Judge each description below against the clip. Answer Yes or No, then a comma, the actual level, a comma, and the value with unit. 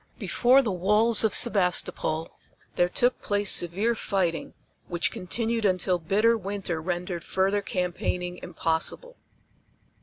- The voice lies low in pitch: No, high, 190 Hz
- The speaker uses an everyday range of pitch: Yes, average, 3.7 semitones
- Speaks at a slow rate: Yes, slow, 115 wpm